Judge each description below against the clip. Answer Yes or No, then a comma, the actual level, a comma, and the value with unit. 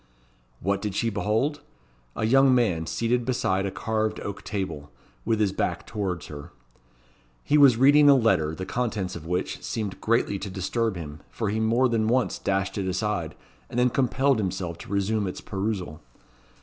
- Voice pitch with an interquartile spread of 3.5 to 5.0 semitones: Yes, average, 3.8 semitones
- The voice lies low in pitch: Yes, low, 105 Hz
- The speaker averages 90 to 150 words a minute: No, average, 175 wpm